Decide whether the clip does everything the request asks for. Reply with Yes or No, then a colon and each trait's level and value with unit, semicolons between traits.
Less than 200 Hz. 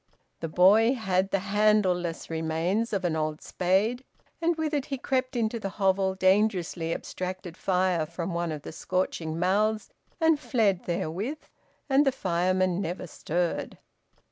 Yes: high, 190 Hz